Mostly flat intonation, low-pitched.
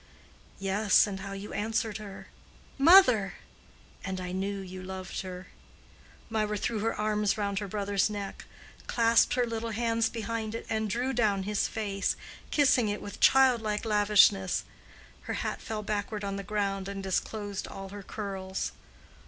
No: narrow, 2.2 semitones; high, 210 Hz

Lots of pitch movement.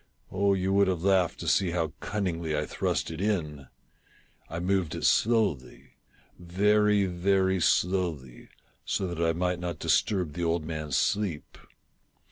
No: average, 3.0 semitones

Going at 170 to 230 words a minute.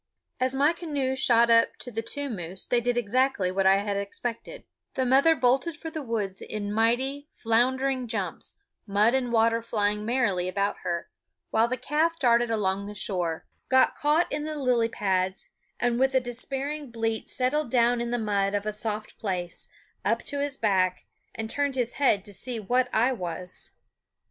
Yes: average, 180 wpm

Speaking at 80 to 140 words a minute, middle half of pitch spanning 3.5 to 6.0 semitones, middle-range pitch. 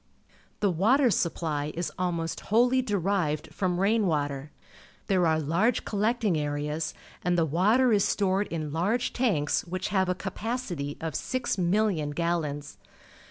Yes: slow, 135 wpm; average, 4.9 semitones; medium, 180 Hz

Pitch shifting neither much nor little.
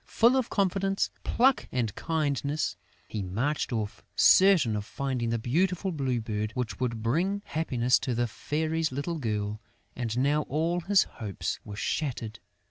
No: wide, 6.4 semitones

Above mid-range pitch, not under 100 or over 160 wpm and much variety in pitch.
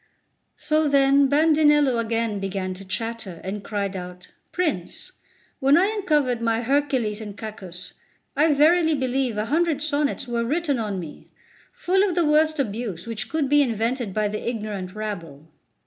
Yes: high, 240 Hz; average, 155 wpm; wide, 6.2 semitones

